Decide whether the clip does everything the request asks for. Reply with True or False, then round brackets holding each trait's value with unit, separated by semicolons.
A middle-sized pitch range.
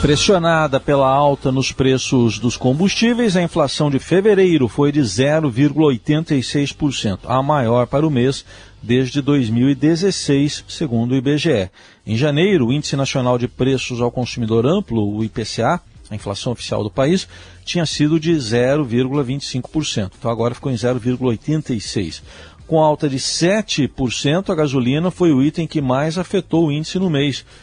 True (4.0 semitones)